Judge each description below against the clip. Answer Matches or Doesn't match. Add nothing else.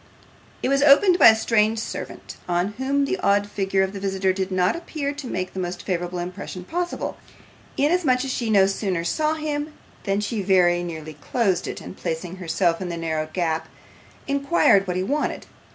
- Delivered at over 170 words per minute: Matches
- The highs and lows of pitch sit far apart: Matches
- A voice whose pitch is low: Doesn't match